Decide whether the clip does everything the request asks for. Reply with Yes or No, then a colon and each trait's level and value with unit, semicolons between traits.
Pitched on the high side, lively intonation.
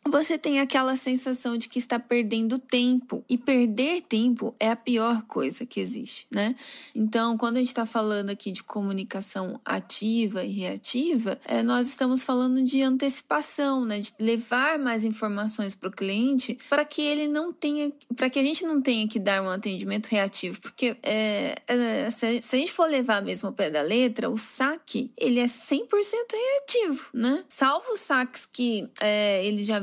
No: high, 245 Hz; average, 3.8 semitones